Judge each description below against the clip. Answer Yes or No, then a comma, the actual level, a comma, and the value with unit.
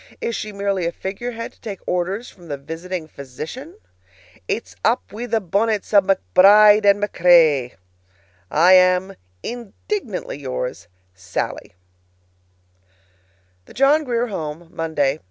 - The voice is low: No, high, 190 Hz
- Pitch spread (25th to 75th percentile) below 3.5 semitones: No, average, 5.1 semitones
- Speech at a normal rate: No, slow, 120 wpm